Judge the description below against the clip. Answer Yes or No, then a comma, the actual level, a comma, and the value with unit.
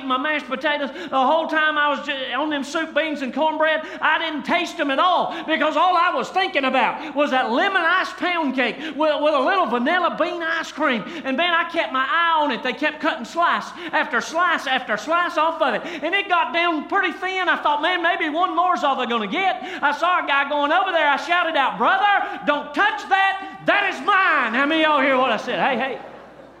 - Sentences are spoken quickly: Yes, fast, 230 wpm